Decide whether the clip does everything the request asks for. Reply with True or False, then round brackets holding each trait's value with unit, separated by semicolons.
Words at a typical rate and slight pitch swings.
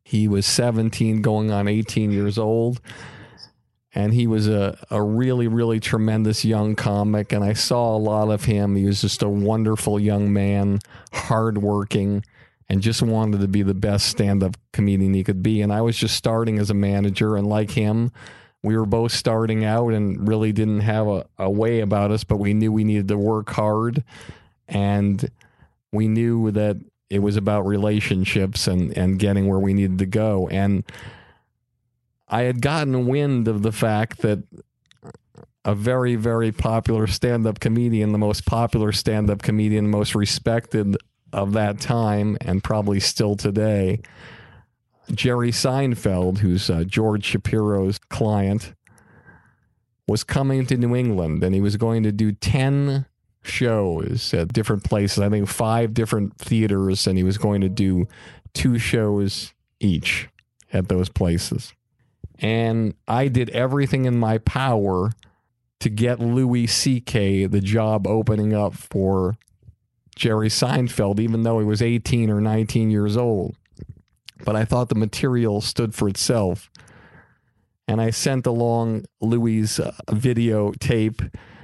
True (155 wpm; 2.2 semitones)